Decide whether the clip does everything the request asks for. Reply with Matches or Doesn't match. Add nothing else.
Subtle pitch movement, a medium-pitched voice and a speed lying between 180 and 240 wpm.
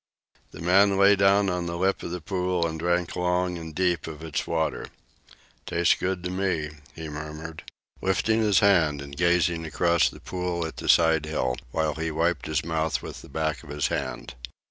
Doesn't match